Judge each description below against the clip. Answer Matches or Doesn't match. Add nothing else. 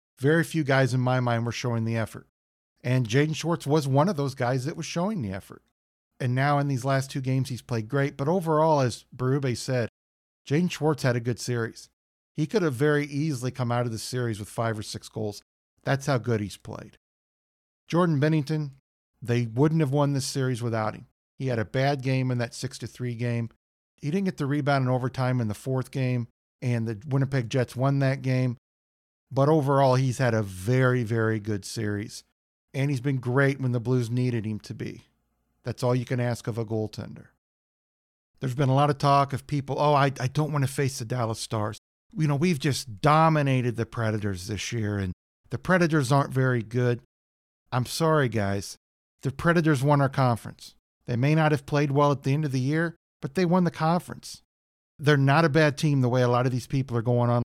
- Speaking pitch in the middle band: Doesn't match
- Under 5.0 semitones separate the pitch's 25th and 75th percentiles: Matches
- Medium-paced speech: Doesn't match